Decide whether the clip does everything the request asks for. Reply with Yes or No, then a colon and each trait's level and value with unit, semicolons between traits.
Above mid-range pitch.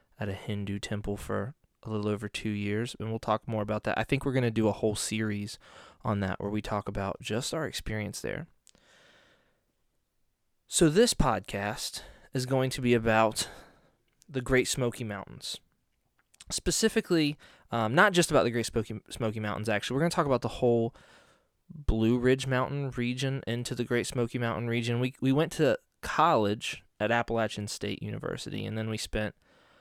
No: low, 115 Hz